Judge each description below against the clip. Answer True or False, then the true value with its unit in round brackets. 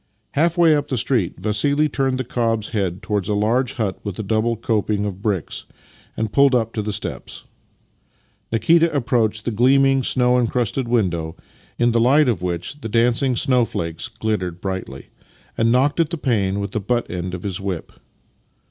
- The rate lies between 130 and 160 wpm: False (175 wpm)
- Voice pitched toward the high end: False (115 Hz)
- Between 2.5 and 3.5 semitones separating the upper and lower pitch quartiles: False (4.3 semitones)